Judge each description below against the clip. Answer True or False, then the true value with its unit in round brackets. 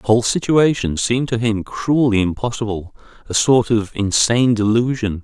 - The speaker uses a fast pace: False (135 wpm)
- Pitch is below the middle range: True (115 Hz)